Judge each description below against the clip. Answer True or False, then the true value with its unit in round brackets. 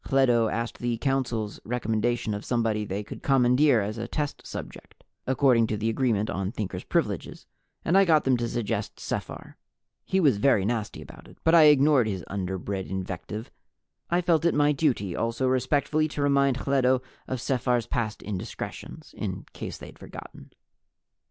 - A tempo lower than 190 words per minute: True (165 wpm)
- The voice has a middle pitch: False (120 Hz)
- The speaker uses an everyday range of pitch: True (4.3 semitones)